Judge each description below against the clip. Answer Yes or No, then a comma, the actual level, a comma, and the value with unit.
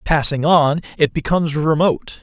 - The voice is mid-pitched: Yes, medium, 155 Hz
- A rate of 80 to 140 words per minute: Yes, slow, 135 wpm